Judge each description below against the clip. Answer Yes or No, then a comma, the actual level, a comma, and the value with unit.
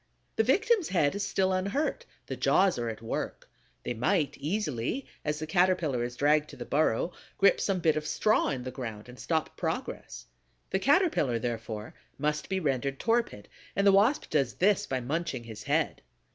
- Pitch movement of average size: No, wide, 7.9 semitones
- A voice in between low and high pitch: Yes, medium, 155 Hz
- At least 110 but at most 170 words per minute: No, average, 180 wpm